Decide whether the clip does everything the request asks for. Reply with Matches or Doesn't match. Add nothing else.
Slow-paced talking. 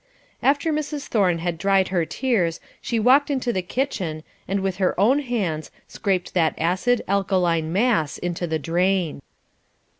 Doesn't match